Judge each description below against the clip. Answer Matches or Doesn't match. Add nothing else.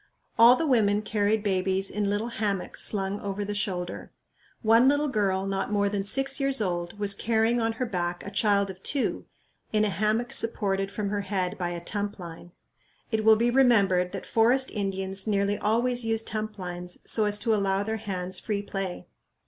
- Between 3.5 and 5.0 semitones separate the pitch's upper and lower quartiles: Doesn't match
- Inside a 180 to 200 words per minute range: Matches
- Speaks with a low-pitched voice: Doesn't match